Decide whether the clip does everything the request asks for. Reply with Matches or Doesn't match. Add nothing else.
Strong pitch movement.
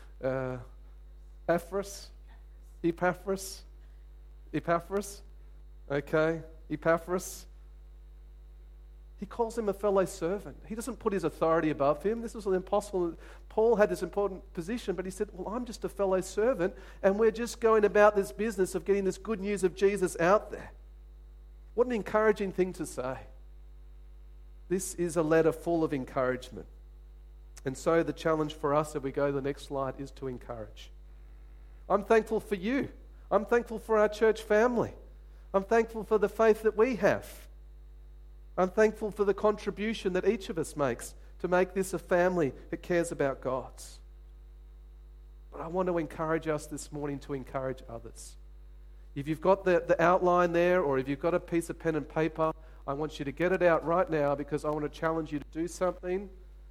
Matches